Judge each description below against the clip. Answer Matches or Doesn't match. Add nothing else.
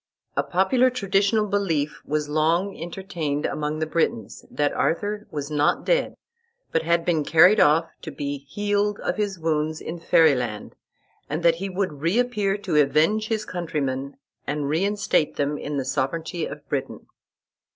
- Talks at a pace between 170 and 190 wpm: Doesn't match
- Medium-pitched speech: Matches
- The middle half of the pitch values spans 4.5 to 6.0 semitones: Matches